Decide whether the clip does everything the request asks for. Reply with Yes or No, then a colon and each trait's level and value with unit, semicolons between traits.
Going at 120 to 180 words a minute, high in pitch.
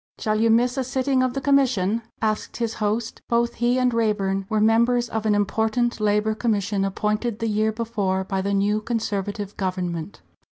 Yes: average, 175 wpm; high, 220 Hz